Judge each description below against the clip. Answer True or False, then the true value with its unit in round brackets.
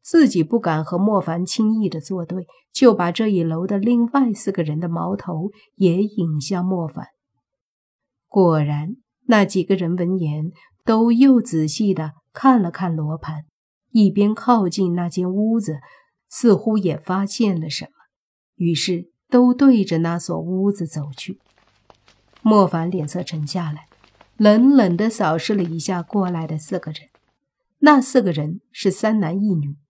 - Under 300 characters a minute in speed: True (215 characters per minute)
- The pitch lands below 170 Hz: False (185 Hz)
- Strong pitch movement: False (4.4 semitones)